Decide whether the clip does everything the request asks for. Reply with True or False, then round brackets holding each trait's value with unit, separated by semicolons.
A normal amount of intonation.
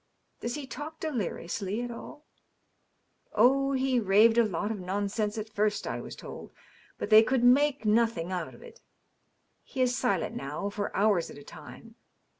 True (4.1 semitones)